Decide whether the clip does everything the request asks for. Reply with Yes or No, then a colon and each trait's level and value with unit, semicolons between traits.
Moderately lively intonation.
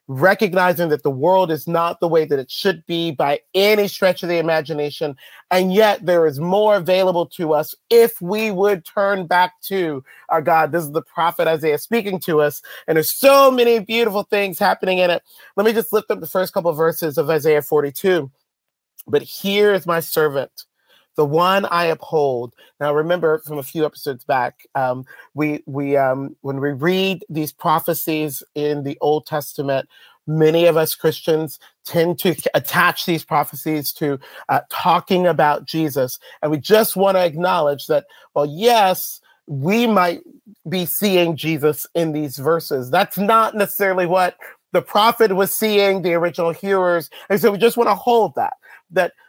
Yes: average, 4.3 semitones